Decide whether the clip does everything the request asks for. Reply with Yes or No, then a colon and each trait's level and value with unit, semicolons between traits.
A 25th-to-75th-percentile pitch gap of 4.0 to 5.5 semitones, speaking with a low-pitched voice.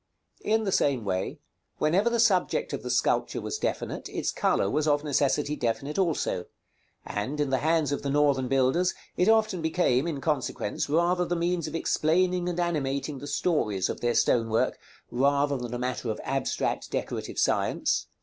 No: average, 5.0 semitones; medium, 150 Hz